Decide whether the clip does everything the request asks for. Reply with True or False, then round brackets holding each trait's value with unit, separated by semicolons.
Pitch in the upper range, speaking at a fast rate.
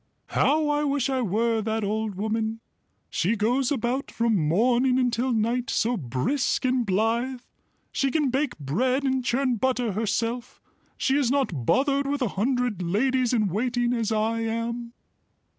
False (240 Hz; 155 wpm)